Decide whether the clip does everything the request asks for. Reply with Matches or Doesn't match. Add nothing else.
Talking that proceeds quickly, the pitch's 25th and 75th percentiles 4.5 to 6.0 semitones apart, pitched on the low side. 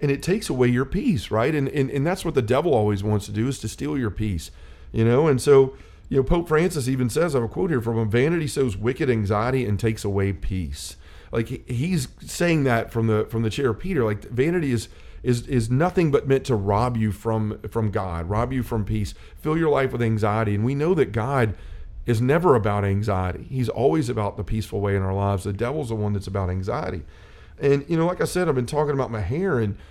Matches